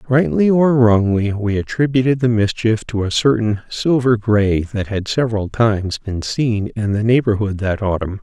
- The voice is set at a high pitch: No, low, 110 Hz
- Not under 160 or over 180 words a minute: Yes, average, 170 wpm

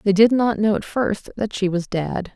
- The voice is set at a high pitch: Yes, high, 205 Hz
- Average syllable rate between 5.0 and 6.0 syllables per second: No, 4.6 syllables/s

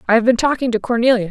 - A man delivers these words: No, female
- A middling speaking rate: No, fast, 275 wpm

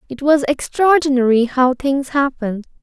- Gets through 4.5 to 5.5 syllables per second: Yes, 4.9 syllables/s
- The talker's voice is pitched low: No, very high, 270 Hz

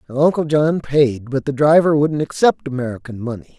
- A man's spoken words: Yes, male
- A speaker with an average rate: Yes, average, 170 wpm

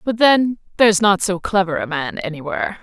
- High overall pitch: Yes, high, 195 Hz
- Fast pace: Yes, fast, 215 wpm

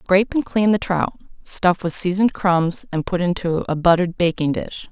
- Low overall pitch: No, medium, 180 Hz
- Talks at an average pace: Yes, average, 195 wpm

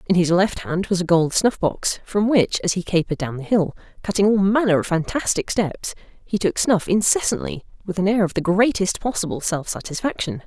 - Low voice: No, high, 190 Hz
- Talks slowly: No, fast, 205 wpm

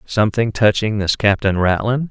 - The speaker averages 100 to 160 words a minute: Yes, average, 140 wpm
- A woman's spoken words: No, male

